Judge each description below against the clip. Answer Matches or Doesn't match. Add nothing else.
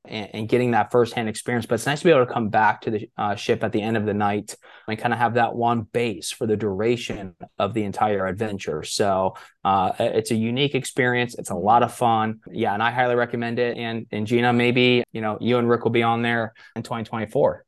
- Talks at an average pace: Doesn't match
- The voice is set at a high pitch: Doesn't match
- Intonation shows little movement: Matches